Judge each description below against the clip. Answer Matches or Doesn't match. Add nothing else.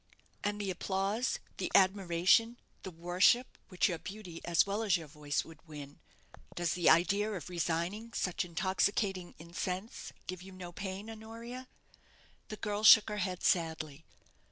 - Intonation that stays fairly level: Doesn't match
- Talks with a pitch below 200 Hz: Matches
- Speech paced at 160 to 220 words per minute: Doesn't match